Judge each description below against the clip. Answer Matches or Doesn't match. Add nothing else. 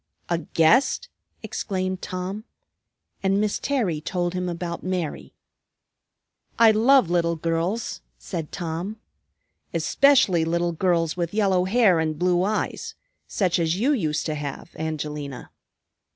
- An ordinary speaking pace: Doesn't match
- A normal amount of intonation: Matches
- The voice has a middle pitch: Matches